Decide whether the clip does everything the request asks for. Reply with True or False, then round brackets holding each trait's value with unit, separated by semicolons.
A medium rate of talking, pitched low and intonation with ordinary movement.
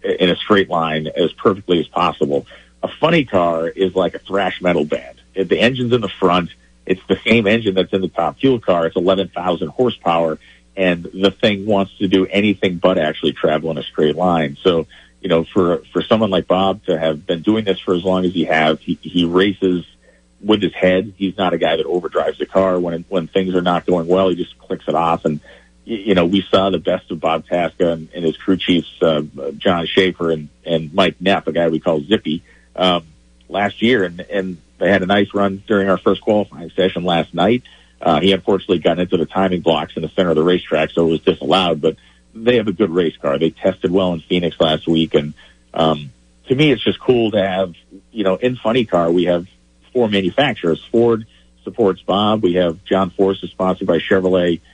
False (220 wpm; 90 Hz; 3.1 semitones)